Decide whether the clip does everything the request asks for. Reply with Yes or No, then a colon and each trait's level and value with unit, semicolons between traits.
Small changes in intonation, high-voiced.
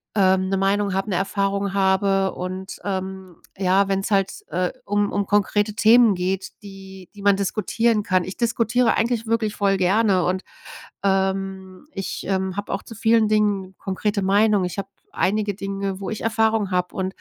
Yes: narrow, 1.7 semitones; high, 195 Hz